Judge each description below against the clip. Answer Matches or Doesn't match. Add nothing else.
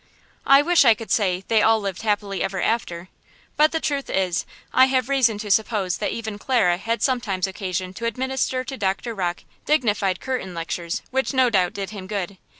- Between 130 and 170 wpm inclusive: Doesn't match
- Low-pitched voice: Doesn't match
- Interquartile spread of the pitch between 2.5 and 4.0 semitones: Doesn't match